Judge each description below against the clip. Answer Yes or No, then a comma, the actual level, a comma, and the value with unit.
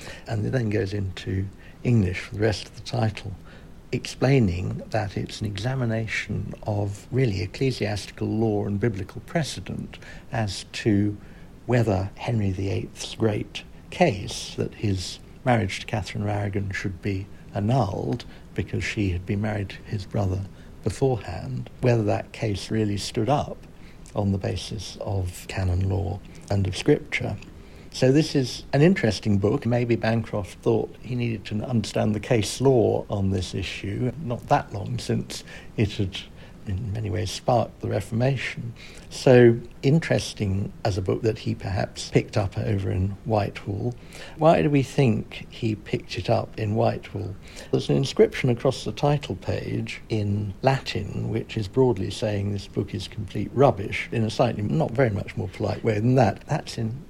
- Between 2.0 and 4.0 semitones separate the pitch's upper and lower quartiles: Yes, average, 3.4 semitones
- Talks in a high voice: No, low, 105 Hz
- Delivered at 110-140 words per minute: No, average, 155 wpm